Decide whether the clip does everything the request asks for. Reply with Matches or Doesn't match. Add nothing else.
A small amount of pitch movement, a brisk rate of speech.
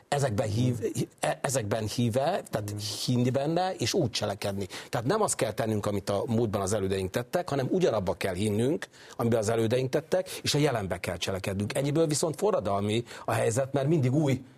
Doesn't match